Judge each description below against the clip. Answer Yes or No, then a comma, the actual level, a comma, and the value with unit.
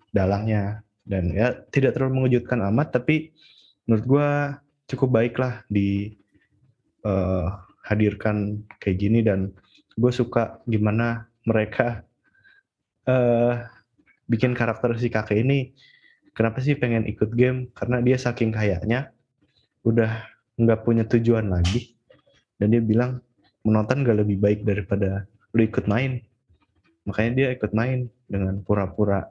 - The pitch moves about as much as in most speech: Yes, average, 3.3 semitones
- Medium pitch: No, low, 115 Hz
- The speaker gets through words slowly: No, average, 125 wpm